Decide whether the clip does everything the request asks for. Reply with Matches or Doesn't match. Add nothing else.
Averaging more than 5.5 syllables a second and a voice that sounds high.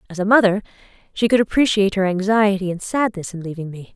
Matches